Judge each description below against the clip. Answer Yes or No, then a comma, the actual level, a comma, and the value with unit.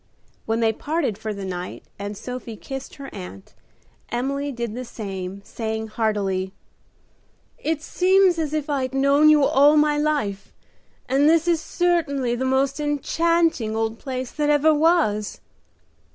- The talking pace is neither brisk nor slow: Yes, average, 145 wpm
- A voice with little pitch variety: No, wide, 5.5 semitones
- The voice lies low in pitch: No, very high, 270 Hz